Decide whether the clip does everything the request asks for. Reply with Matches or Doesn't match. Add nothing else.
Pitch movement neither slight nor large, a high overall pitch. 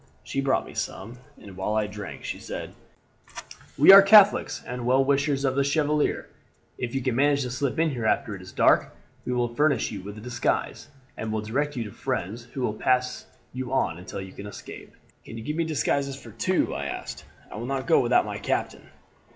Doesn't match